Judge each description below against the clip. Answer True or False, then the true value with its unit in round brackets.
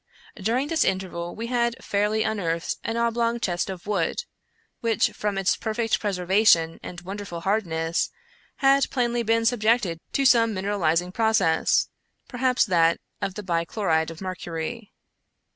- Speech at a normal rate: True (145 wpm)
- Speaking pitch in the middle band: False (205 Hz)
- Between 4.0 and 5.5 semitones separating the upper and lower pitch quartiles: True (5.0 semitones)